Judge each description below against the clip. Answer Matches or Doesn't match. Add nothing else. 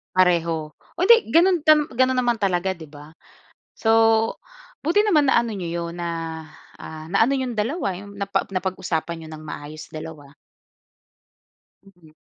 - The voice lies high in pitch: Matches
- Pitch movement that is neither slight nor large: Doesn't match